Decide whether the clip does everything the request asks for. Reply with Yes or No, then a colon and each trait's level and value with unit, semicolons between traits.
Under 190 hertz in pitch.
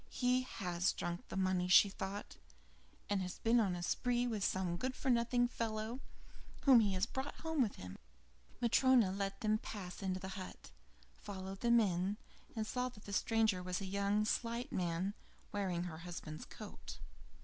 No: high, 200 Hz